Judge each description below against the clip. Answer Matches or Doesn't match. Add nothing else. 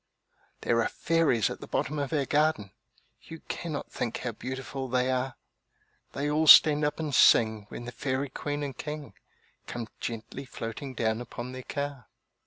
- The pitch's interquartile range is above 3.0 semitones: Matches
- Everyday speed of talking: Matches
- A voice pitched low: Matches